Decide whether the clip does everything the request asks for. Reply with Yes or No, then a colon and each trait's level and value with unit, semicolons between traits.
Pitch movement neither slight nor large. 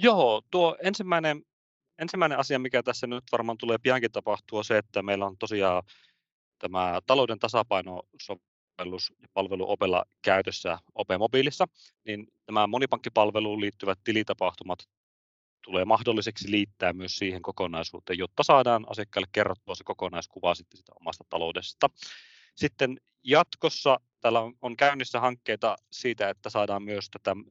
Yes: average, 4.7 semitones